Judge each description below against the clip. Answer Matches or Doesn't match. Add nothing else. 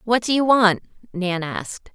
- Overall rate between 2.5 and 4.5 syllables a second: Matches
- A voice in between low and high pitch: Doesn't match